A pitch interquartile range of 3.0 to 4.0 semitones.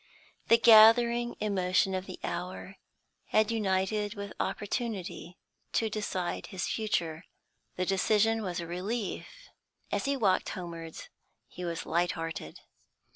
Yes: average, 3.5 semitones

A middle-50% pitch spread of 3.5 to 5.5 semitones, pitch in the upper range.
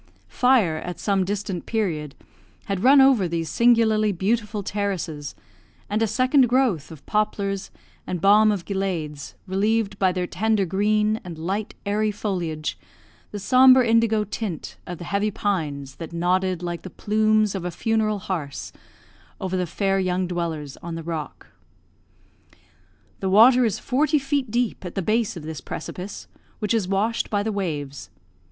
Yes: average, 3.8 semitones; high, 200 Hz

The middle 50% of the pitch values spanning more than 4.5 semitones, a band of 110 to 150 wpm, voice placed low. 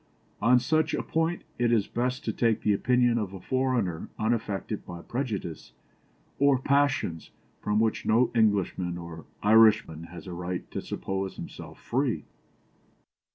Yes: average, 5.2 semitones; average, 145 wpm; low, 110 Hz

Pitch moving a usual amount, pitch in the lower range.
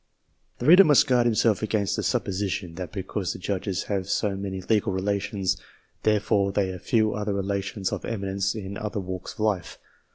No: narrow, 2.0 semitones; low, 100 Hz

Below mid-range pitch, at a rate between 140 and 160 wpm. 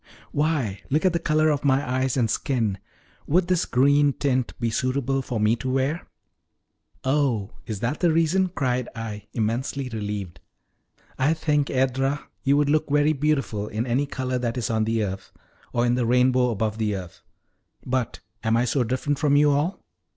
No: low, 130 Hz; average, 180 wpm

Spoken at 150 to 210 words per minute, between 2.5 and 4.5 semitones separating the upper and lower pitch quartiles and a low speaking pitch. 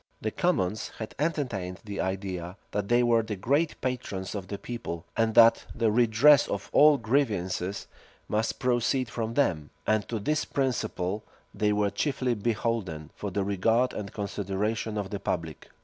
Yes: average, 165 wpm; average, 3.8 semitones; low, 110 Hz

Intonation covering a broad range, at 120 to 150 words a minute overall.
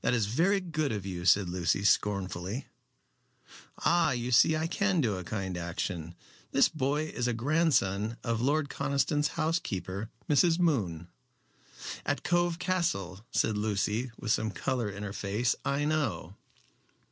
Yes: wide, 7.9 semitones; average, 145 wpm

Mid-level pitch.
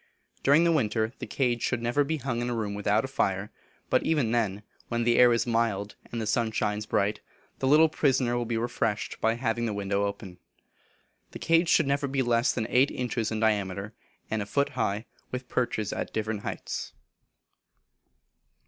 No: low, 115 Hz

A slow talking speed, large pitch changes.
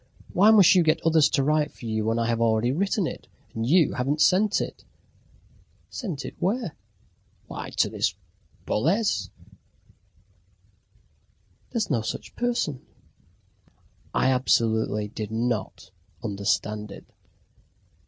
Yes: slow, 125 wpm; wide, 8.3 semitones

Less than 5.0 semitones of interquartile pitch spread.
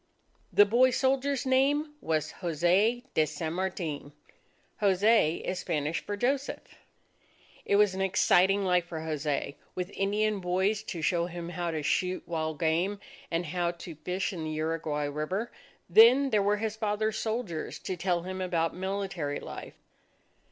Yes: average, 4.2 semitones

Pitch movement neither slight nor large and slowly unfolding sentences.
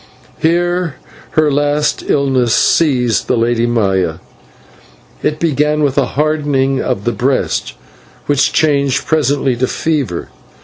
Yes: average, 3.6 semitones; slow, 120 wpm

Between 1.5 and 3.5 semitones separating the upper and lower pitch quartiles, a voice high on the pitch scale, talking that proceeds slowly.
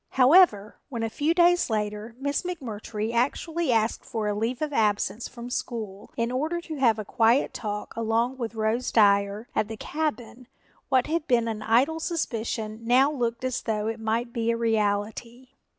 No: average, 3.2 semitones; high, 230 Hz; average, 175 wpm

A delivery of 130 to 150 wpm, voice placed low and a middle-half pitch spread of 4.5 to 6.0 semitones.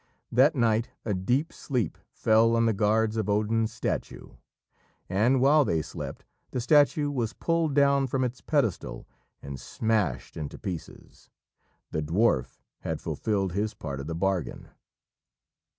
Yes: average, 140 wpm; low, 110 Hz; average, 5.2 semitones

